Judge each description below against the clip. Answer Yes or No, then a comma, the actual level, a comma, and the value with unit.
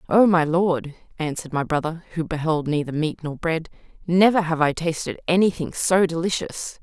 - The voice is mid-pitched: Yes, medium, 165 Hz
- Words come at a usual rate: Yes, average, 165 wpm